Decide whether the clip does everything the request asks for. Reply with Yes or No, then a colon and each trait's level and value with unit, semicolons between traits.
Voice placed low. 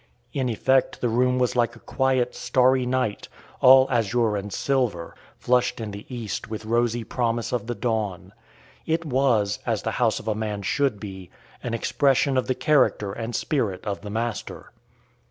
Yes: low, 120 Hz